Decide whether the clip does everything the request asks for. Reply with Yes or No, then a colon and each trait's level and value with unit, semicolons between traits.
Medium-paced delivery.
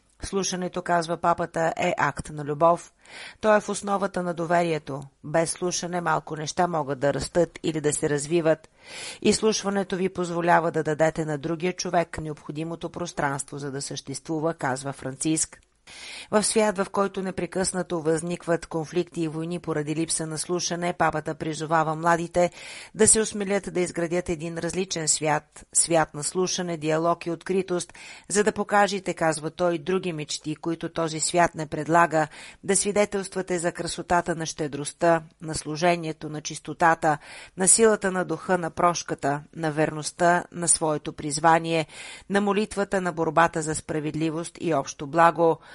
Yes: average, 145 wpm